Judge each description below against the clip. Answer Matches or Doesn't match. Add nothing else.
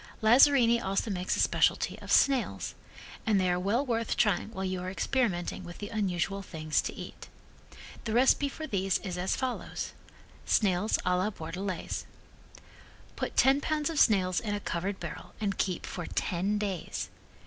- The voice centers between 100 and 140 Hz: Doesn't match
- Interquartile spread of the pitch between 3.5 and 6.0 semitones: Matches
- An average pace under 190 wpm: Matches